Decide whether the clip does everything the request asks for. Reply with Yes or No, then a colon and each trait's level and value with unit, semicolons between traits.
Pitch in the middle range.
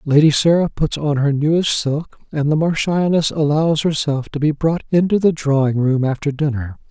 Yes: medium, 150 Hz